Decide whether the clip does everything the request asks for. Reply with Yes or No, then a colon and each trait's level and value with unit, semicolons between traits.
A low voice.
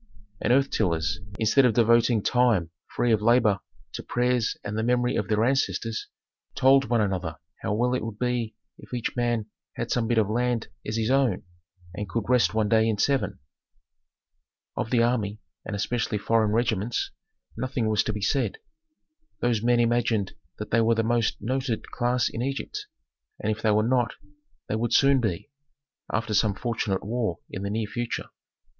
Yes: low, 115 Hz